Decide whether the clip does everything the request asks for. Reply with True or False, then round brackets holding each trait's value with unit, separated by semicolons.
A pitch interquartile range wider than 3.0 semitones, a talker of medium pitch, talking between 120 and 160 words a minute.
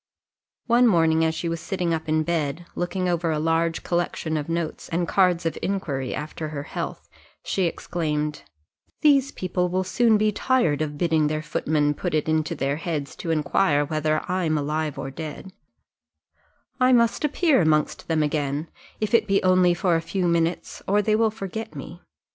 False (3.4 semitones; 165 Hz; 180 wpm)